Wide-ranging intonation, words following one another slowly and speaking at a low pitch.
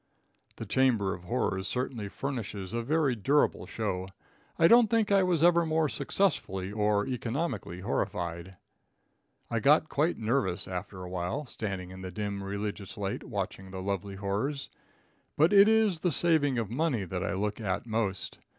No: wide, 7.3 semitones; average, 160 wpm; low, 110 Hz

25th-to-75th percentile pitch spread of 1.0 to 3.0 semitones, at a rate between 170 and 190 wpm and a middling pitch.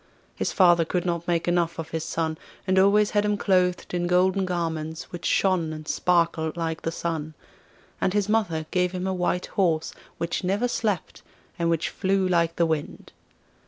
Yes: narrow, 2.4 semitones; average, 180 wpm; medium, 175 Hz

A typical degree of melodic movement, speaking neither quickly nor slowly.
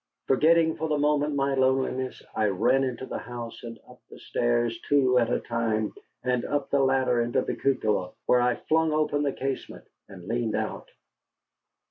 Yes: average, 3.2 semitones; average, 175 wpm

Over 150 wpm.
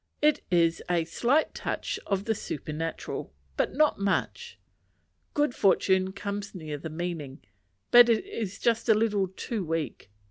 No: average, 140 wpm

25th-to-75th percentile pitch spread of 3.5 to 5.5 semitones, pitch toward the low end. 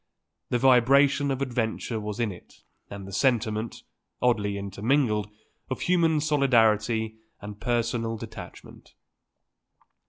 Yes: average, 3.9 semitones; low, 115 Hz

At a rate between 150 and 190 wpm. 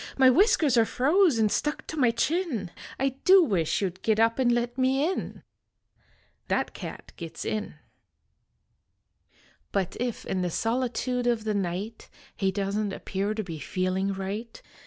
Yes: average, 160 wpm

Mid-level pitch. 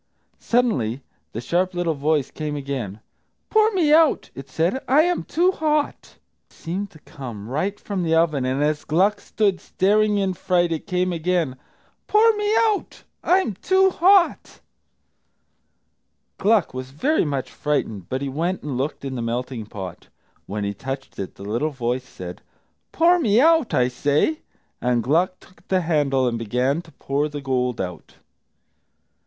Yes: medium, 155 Hz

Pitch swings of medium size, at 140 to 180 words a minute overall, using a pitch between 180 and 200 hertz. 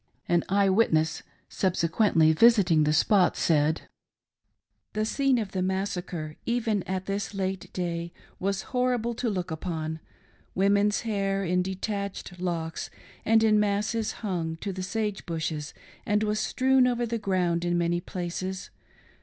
Yes: average, 3.6 semitones; average, 145 wpm; high, 190 Hz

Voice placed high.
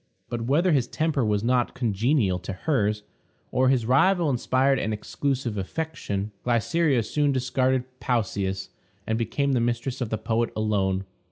No: low, 120 Hz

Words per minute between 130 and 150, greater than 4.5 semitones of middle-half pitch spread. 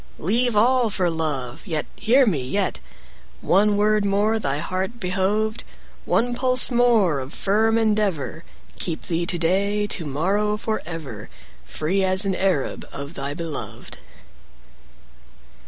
Yes: average, 140 wpm; average, 4.9 semitones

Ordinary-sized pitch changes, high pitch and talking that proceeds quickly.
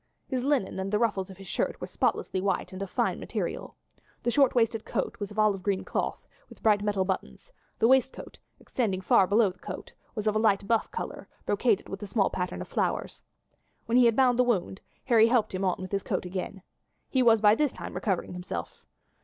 Yes: average, 3.5 semitones; high, 210 Hz; fast, 210 wpm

